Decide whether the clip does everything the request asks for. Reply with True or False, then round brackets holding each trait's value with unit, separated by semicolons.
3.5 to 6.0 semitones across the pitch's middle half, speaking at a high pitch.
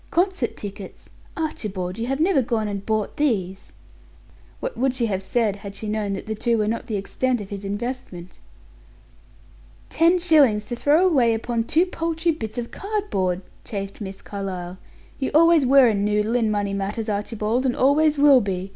True (5.6 semitones; 225 Hz)